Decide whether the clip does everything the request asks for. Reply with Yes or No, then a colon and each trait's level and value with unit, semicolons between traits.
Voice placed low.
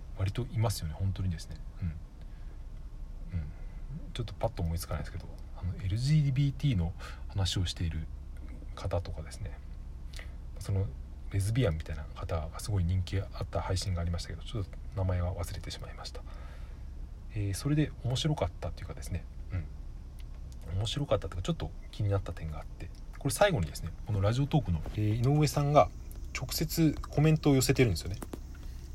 Yes: very low, 90 Hz